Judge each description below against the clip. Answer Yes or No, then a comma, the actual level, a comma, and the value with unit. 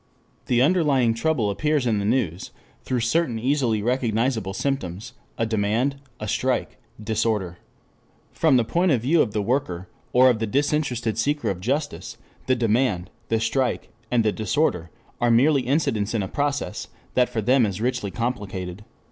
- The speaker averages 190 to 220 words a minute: No, average, 160 wpm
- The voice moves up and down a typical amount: Yes, average, 4.2 semitones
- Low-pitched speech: Yes, low, 120 Hz